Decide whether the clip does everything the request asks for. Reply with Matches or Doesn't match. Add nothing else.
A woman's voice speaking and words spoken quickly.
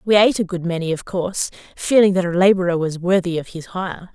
Matches